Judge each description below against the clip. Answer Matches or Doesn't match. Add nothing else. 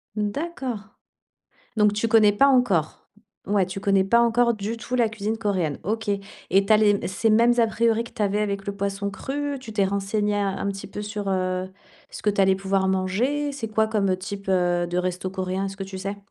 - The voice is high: Matches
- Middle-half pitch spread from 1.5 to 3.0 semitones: Matches